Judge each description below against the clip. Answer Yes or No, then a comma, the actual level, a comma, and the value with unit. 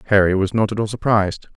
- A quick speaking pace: Yes, fast, 230 wpm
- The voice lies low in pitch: Yes, low, 105 Hz